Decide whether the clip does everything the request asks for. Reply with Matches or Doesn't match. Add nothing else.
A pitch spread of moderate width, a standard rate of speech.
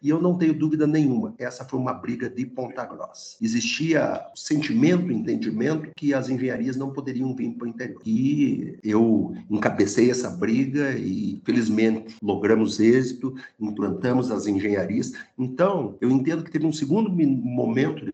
Matches